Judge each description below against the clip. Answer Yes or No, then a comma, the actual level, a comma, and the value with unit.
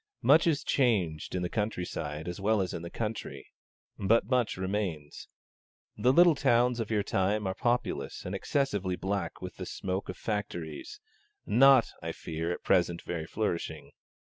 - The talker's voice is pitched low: Yes, low, 100 Hz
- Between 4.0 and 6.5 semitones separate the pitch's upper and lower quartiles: Yes, average, 5.1 semitones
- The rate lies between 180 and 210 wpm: No, average, 165 wpm